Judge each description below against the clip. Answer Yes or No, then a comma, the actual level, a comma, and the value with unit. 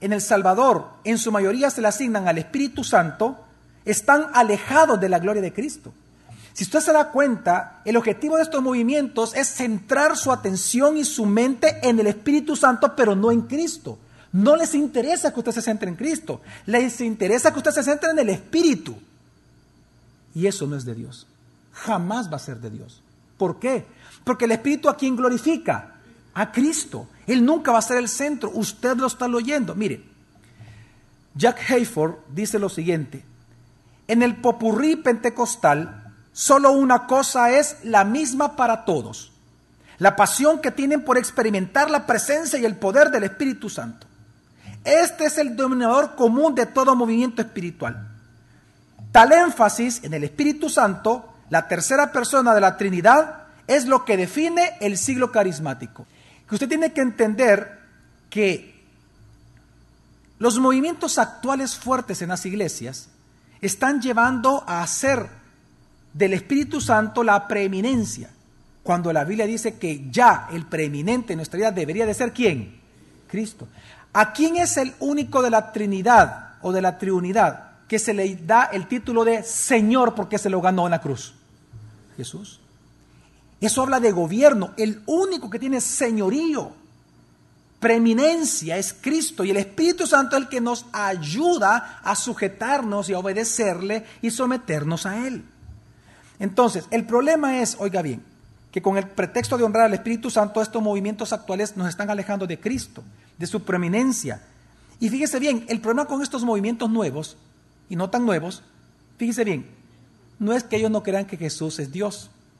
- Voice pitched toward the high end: Yes, high, 220 Hz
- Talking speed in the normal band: Yes, average, 160 wpm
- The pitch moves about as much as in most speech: No, wide, 6.1 semitones